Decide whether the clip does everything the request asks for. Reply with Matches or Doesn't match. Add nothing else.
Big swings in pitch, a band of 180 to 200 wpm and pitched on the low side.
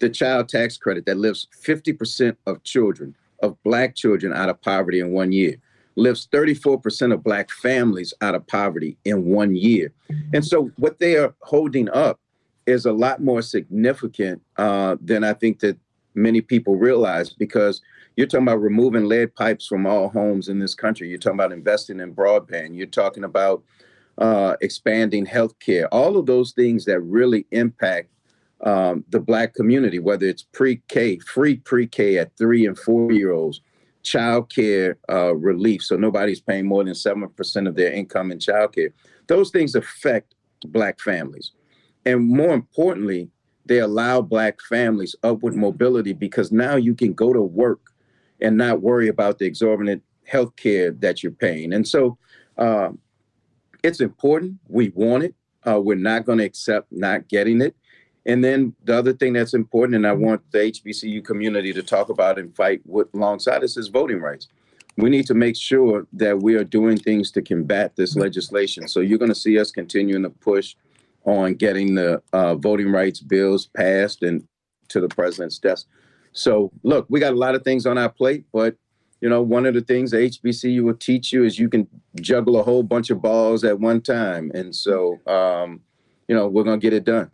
Doesn't match